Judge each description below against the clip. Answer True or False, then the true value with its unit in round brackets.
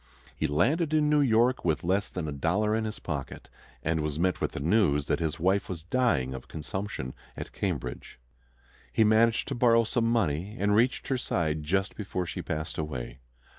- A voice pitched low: True (95 Hz)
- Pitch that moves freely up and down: True (6.7 semitones)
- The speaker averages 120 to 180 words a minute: False (190 wpm)